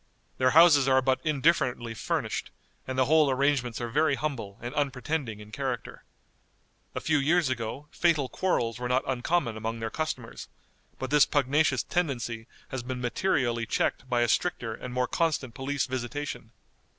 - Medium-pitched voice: No, low, 130 Hz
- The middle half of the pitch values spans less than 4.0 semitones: Yes, average, 3.6 semitones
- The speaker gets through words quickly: No, average, 160 wpm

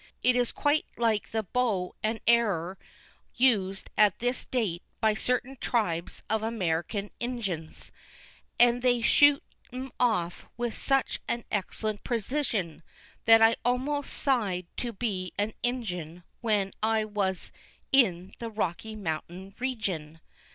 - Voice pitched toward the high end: Yes, high, 220 Hz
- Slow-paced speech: Yes, slow, 130 wpm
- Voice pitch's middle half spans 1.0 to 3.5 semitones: No, average, 4.5 semitones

